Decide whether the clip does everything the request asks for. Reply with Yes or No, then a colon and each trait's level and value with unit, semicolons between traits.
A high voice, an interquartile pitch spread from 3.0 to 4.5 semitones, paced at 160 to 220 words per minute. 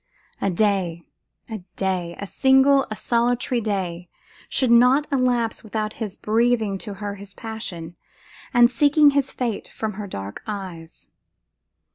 No: high, 215 Hz; average, 4.2 semitones; slow, 135 wpm